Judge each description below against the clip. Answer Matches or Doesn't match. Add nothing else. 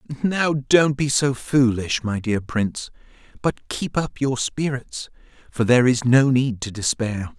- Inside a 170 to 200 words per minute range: Doesn't match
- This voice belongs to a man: Matches